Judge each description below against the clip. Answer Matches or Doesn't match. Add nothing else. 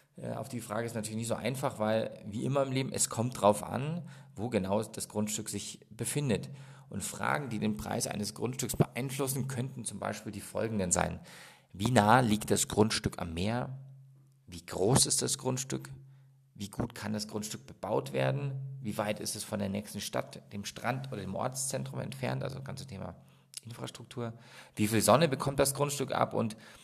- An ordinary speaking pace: Matches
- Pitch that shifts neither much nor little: Matches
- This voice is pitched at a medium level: Doesn't match